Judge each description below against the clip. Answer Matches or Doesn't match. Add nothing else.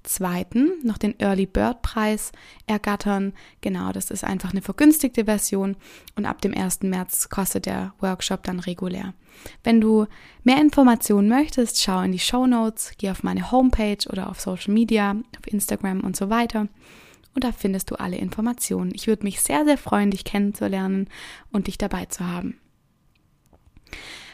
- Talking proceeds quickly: Doesn't match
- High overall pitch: Matches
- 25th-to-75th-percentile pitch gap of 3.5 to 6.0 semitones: Doesn't match